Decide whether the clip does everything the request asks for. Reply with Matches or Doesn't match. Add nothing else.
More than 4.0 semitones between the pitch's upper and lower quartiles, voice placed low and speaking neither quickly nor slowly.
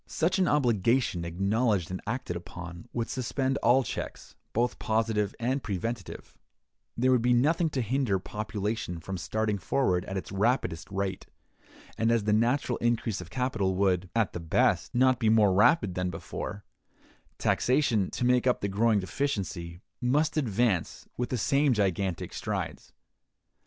Matches